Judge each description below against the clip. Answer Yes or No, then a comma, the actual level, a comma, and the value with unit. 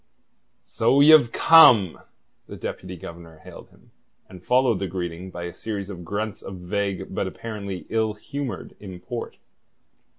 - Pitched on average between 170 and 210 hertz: No, low, 100 Hz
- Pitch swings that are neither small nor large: Yes, average, 4.0 semitones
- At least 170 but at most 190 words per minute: No, average, 140 wpm